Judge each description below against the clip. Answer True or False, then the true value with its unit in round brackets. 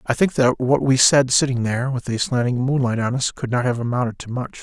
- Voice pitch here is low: True (125 Hz)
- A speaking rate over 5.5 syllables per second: True (5.8 syllables/s)